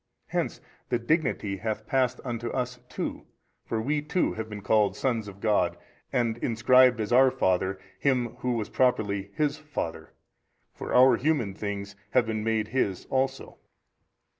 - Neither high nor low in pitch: No, low, 115 Hz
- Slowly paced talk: No, average, 155 wpm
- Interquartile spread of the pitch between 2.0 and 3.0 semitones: No, average, 3.6 semitones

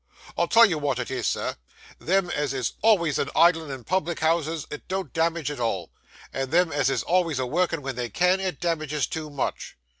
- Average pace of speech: No, fast, 210 wpm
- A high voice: No, medium, 160 Hz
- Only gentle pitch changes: No, average, 4.2 semitones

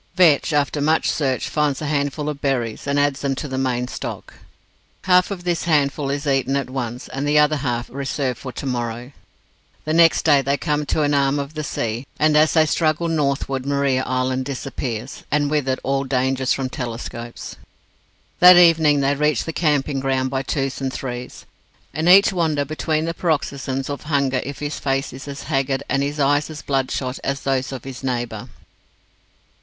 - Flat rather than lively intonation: Yes, narrow, 2.3 semitones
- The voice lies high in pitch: No, medium, 140 Hz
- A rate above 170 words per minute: Yes, average, 185 wpm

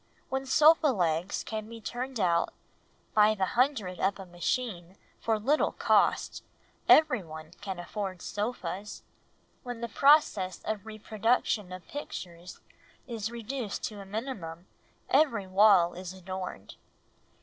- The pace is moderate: No, slow, 125 wpm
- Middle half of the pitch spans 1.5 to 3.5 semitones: No, average, 4.7 semitones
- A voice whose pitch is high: Yes, high, 210 Hz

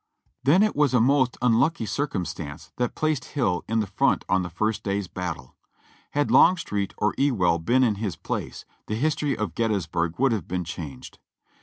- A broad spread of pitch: Yes, wide, 6.8 semitones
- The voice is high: No, low, 110 Hz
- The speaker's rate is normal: Yes, average, 175 wpm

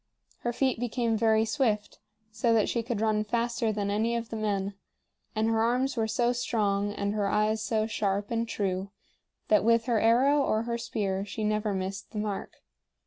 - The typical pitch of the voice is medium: No, high, 220 Hz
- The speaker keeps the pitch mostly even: Yes, narrow, 2.0 semitones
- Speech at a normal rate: Yes, average, 190 wpm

